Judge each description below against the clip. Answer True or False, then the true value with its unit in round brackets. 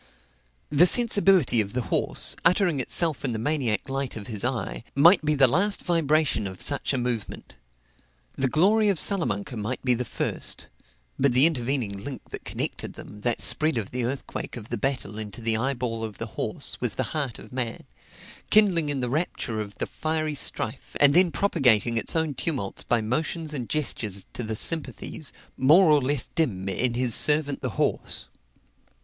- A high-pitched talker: False (130 Hz)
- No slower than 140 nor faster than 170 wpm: False (180 wpm)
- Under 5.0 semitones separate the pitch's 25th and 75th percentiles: False (5.3 semitones)